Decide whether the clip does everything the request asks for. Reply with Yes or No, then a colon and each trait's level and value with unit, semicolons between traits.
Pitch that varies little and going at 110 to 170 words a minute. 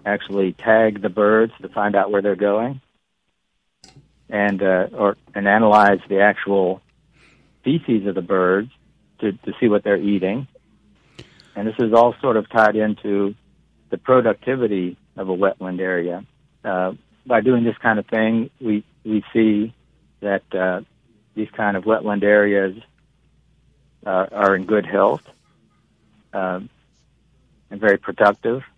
Yes: narrow, 2.2 semitones; average, 140 wpm